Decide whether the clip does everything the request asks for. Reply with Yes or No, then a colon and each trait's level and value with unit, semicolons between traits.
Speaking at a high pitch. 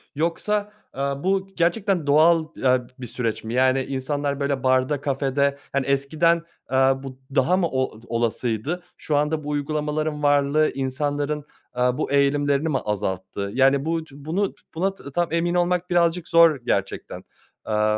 No: medium, 145 Hz